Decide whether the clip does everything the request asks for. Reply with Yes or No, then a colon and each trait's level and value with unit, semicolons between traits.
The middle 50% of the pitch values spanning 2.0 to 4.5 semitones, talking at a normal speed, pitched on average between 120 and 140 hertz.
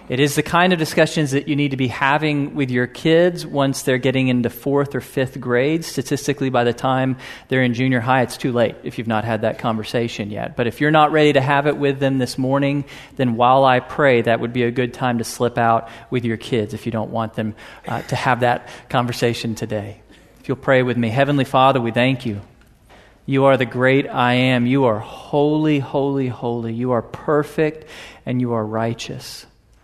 No: average, 2.8 semitones; fast, 215 wpm; low, 130 Hz